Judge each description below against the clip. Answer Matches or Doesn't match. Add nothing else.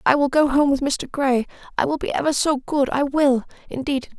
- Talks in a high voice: Matches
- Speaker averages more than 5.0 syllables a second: Matches